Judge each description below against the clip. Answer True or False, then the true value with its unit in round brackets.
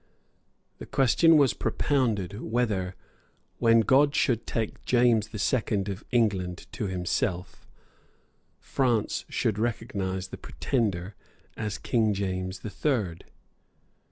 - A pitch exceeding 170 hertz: False (110 Hz)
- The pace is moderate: False (110 wpm)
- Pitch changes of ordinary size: True (4.3 semitones)